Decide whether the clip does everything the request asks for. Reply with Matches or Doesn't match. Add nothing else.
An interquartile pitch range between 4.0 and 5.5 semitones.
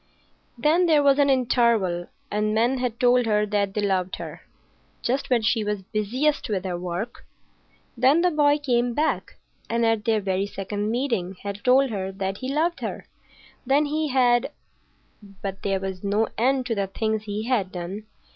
Matches